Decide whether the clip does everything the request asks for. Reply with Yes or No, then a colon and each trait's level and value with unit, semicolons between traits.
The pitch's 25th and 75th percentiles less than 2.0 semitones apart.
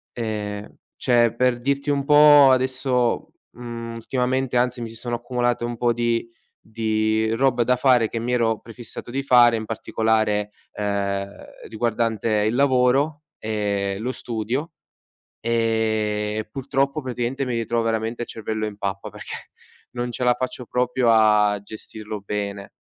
No: narrow, 2.4 semitones